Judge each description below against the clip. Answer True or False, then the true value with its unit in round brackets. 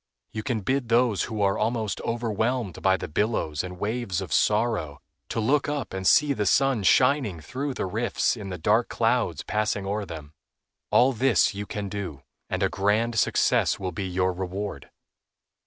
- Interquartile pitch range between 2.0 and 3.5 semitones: False (4.0 semitones)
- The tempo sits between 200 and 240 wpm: False (175 wpm)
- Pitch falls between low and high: False (105 Hz)